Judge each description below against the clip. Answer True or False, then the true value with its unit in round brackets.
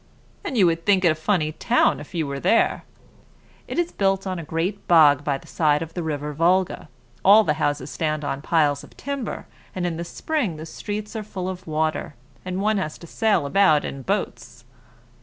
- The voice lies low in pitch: False (170 Hz)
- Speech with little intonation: False (4.4 semitones)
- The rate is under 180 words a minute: False (205 wpm)